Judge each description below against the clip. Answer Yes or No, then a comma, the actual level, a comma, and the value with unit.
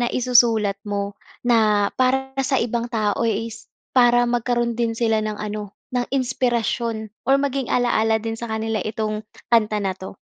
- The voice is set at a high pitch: Yes, high, 230 Hz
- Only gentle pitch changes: Yes, narrow, 2.2 semitones